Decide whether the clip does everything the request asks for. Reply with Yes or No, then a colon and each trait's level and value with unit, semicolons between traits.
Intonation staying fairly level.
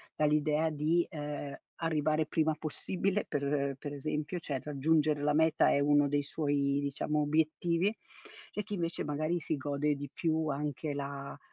Yes: narrow, 1.8 semitones